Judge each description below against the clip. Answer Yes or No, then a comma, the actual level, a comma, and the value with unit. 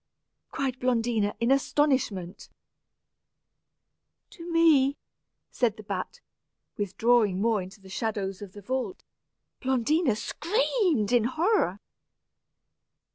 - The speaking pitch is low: No, high, 240 Hz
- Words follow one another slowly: Yes, slow, 95 wpm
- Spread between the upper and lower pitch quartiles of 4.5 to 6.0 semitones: Yes, wide, 5.6 semitones